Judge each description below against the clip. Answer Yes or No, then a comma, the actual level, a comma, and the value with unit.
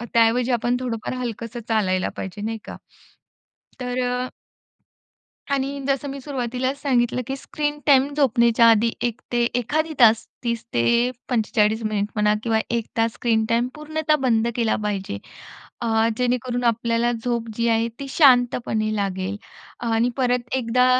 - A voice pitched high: Yes, high, 235 Hz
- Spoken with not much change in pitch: Yes, narrow, 2.1 semitones